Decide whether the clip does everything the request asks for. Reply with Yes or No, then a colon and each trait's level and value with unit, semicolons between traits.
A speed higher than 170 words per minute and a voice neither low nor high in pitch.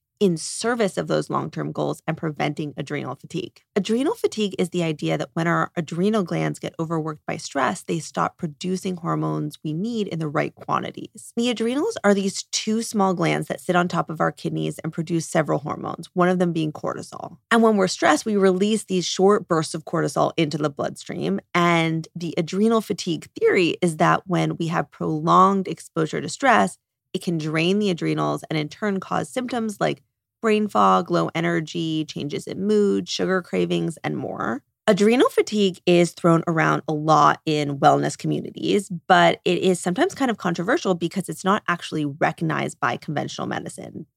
Yes: average, 180 wpm; medium, 175 Hz